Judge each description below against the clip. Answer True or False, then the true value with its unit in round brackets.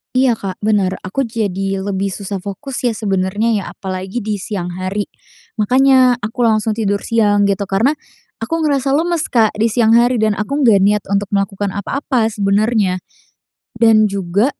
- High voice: True (210 Hz)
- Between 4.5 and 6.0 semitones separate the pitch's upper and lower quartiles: False (3.1 semitones)